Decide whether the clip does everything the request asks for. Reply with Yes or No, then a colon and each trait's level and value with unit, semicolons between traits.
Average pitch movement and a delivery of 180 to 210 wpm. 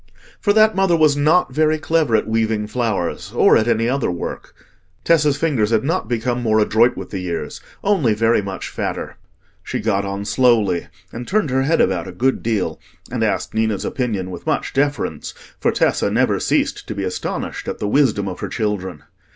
No: wide, 5.9 semitones; average, 185 wpm